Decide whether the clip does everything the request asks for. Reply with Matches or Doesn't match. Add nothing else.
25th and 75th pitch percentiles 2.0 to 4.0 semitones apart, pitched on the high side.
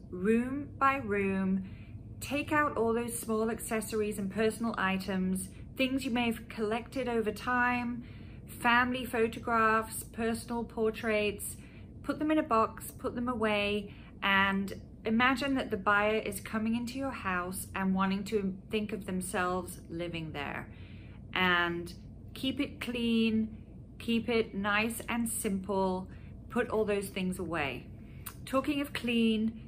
Matches